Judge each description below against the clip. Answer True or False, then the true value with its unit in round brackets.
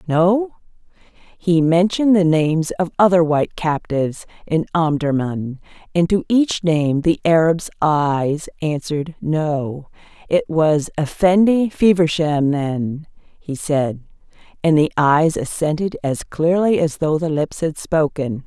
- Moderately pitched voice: True (160 Hz)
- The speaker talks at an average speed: False (125 wpm)